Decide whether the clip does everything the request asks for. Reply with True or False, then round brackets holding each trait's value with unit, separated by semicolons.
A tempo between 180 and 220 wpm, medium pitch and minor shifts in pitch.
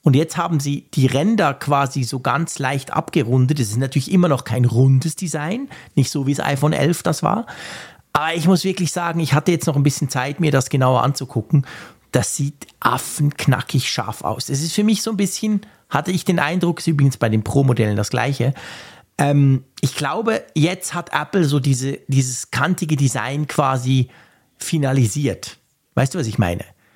False (185 wpm; 145 Hz; 4.0 semitones)